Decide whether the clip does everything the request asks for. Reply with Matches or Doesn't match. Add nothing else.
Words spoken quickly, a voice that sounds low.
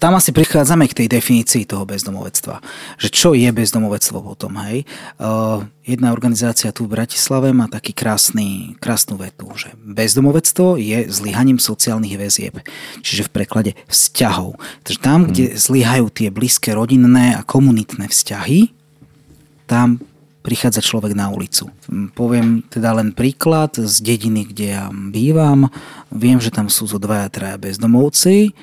Doesn't match